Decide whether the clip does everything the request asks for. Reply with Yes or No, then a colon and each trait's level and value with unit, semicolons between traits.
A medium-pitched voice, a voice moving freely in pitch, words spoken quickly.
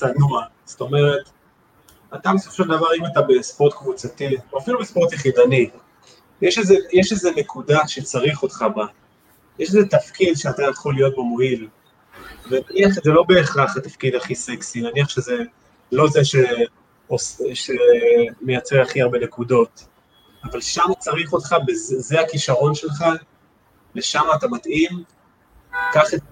No: medium, 155 Hz; wide, 6.4 semitones; average, 130 wpm